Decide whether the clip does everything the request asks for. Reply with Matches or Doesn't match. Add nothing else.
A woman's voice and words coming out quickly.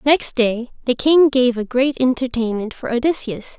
Doesn't match